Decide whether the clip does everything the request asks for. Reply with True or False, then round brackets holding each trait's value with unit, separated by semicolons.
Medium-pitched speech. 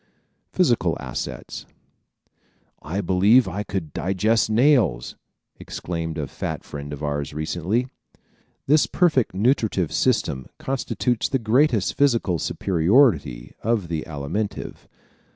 False (95 Hz)